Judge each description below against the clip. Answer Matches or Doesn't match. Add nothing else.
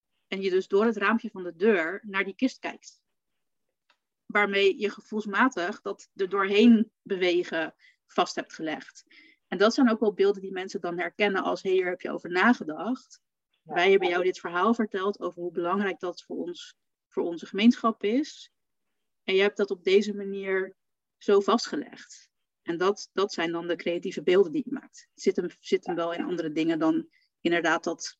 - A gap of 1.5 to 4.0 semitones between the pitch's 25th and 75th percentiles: Doesn't match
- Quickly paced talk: Doesn't match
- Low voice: Doesn't match